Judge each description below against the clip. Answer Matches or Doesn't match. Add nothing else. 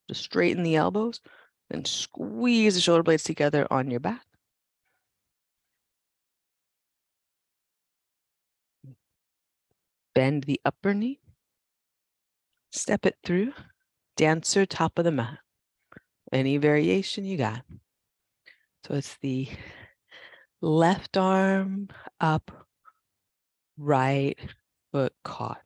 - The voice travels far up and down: Matches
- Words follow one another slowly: Matches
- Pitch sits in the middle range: Matches